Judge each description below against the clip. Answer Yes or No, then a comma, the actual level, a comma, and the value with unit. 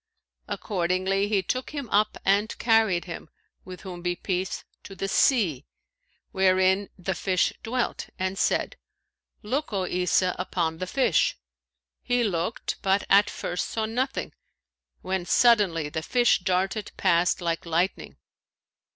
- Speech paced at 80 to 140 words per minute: Yes, slow, 135 wpm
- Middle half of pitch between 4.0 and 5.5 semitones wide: No, average, 3.1 semitones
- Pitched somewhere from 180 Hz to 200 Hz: Yes, high, 190 Hz